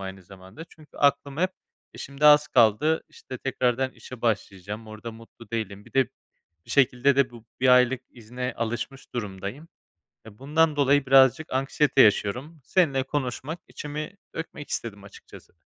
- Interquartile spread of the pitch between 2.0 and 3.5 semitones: No, average, 4.2 semitones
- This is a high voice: No, low, 130 Hz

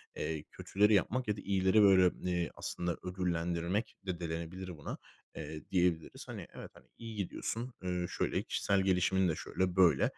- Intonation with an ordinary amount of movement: No, narrow, 2.3 semitones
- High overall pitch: No, very low, 90 Hz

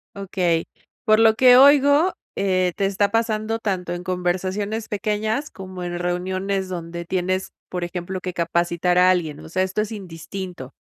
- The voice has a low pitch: No, medium, 185 Hz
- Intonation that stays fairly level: No, average, 3.1 semitones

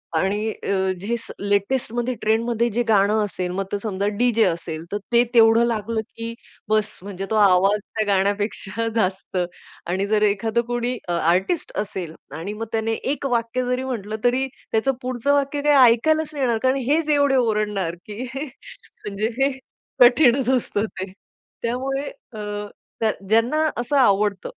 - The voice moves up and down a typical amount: Yes, average, 3.7 semitones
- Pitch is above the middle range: Yes, high, 225 Hz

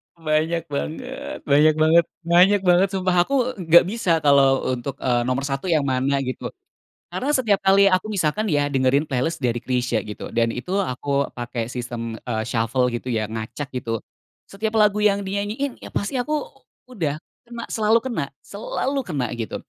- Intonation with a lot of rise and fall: Yes, wide, 7.9 semitones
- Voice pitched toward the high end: No, medium, 155 Hz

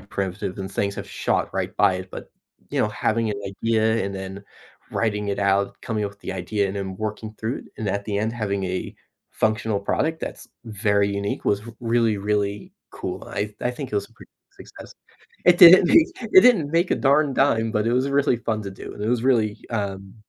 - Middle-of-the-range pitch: No, low, 105 Hz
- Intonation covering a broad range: No, average, 2.8 semitones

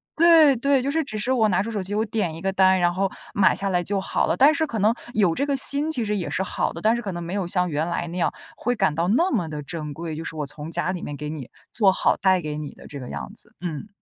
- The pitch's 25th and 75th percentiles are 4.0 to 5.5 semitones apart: Yes, average, 5.2 semitones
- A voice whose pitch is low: No, high, 190 Hz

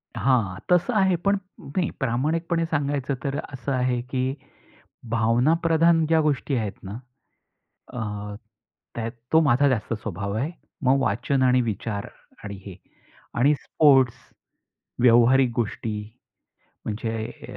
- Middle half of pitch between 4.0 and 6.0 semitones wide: Yes, average, 4.8 semitones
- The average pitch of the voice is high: No, low, 130 Hz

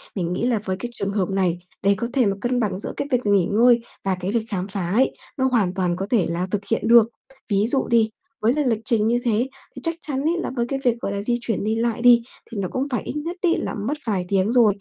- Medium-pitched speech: No, high, 225 Hz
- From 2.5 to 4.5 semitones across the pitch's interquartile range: Yes, average, 3.8 semitones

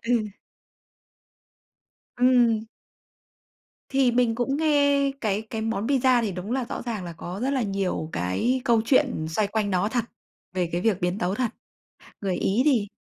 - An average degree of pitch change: Yes, average, 4.5 semitones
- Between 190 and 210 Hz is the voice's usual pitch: No, high, 225 Hz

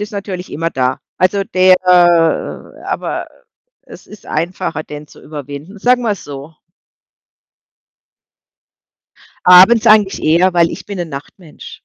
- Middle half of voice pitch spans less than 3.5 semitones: No, average, 4.0 semitones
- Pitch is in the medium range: Yes, medium, 180 Hz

